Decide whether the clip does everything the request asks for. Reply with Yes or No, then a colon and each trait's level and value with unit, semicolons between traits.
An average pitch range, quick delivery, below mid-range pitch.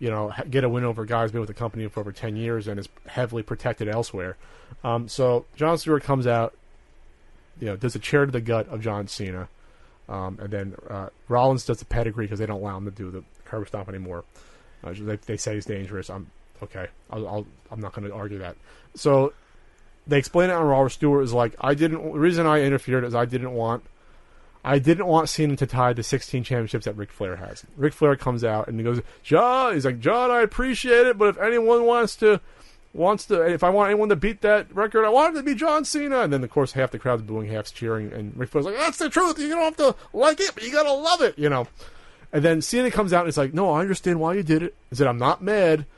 No: wide, 7.8 semitones; fast, 250 wpm; low, 130 Hz